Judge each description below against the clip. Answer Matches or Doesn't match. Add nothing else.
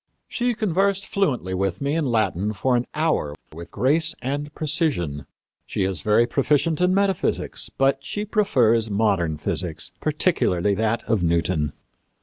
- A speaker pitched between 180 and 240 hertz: Doesn't match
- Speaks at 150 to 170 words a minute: Doesn't match